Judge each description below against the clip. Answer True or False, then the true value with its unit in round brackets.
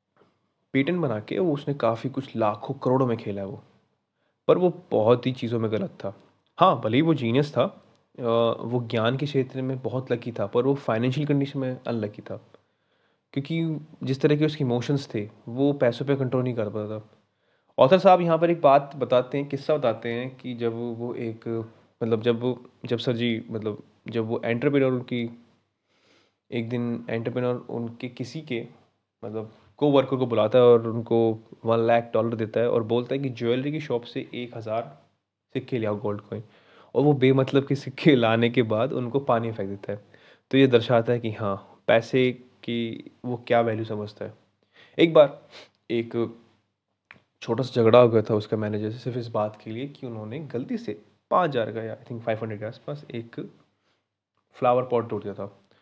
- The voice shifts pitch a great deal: False (2.9 semitones)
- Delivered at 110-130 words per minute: False (190 wpm)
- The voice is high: False (120 Hz)